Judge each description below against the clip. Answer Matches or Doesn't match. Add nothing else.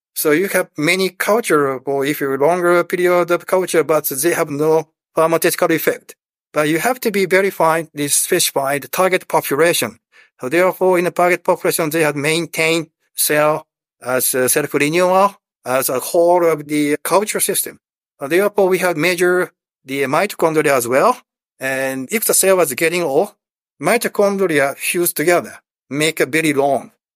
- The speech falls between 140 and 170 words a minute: Matches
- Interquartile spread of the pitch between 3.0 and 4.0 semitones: Matches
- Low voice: Doesn't match